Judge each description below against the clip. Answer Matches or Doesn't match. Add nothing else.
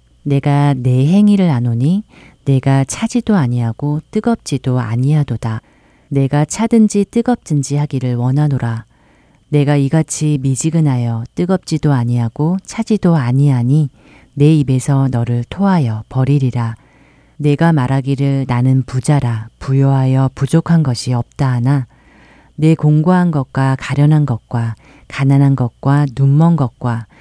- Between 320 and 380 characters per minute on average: Doesn't match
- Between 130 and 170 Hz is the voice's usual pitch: Matches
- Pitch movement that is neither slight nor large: Matches